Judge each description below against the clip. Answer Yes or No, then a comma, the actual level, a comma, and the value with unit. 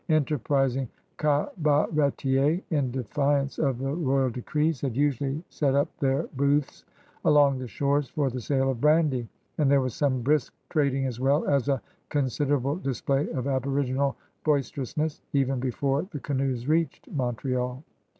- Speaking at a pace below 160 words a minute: Yes, average, 140 wpm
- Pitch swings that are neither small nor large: No, narrow, 1.9 semitones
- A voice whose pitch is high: No, medium, 140 Hz